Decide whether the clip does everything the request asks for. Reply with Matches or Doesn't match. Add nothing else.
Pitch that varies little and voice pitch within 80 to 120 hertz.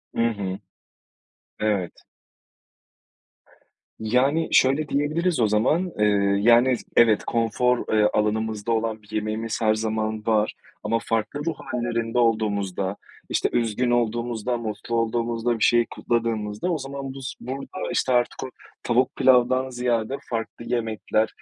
Matches